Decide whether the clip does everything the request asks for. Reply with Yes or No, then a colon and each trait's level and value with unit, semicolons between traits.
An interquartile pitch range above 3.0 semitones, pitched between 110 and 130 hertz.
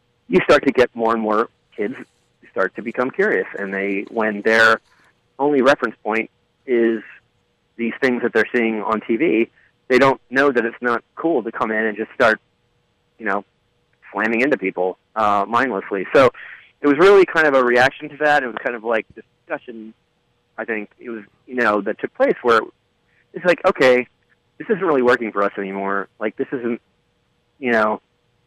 No: narrow, 2.6 semitones; low, 115 Hz